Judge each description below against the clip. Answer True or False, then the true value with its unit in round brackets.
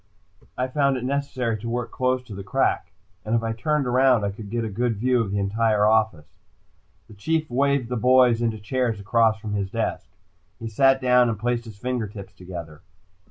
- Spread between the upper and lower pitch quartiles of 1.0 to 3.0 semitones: False (3.4 semitones)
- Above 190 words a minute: True (200 wpm)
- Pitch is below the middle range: True (115 Hz)